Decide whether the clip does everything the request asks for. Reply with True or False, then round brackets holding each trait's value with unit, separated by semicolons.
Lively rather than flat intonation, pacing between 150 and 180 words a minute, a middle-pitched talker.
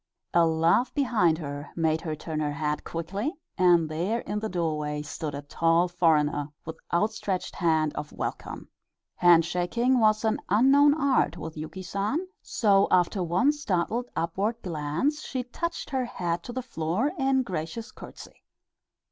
True (6.4 semitones; 155 wpm; 175 Hz)